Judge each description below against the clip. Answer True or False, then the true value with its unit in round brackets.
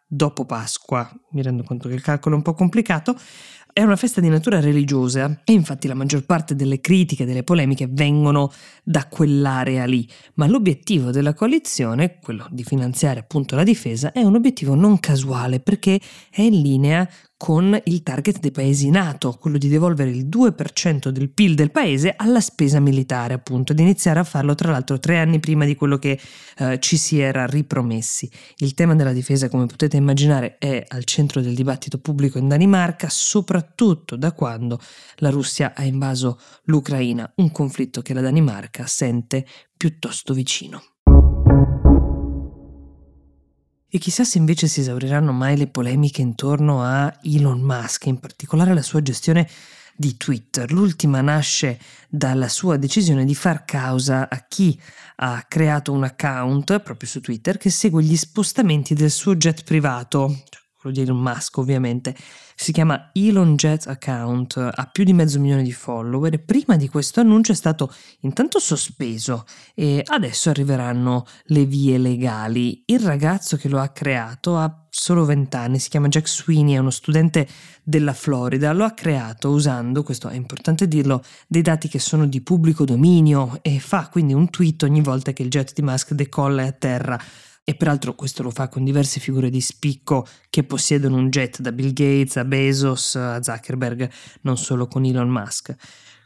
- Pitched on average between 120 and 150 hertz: True (140 Hz)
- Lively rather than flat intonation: False (3.7 semitones)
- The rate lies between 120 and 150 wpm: False (165 wpm)